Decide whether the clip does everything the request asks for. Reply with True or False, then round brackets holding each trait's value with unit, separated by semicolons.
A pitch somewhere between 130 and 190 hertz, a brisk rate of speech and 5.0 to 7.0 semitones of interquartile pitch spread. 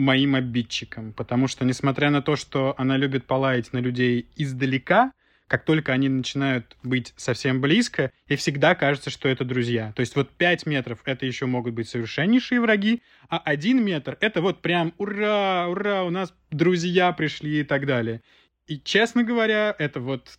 True (140 Hz; 170 wpm; 5.3 semitones)